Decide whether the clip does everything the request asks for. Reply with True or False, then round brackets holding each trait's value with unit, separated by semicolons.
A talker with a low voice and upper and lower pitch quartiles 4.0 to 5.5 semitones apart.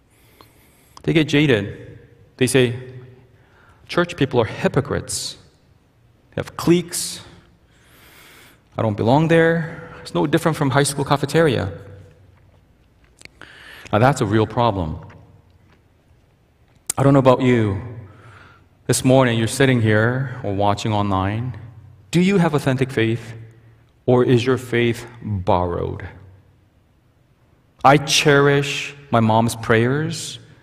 True (120 Hz; 4.5 semitones)